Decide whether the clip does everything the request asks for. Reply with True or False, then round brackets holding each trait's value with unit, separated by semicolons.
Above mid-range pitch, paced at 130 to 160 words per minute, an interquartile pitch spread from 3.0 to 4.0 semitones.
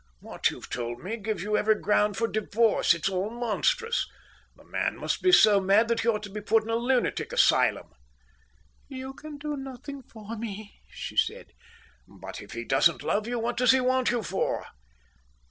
False (225 Hz; 190 wpm; 3.5 semitones)